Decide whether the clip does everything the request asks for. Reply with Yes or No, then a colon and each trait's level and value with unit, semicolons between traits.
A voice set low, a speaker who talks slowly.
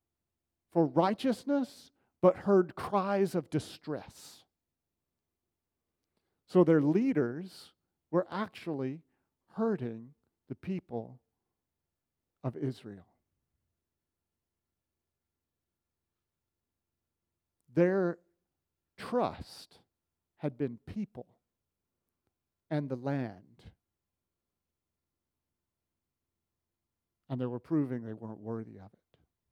Yes: low, 105 Hz; slow, 70 wpm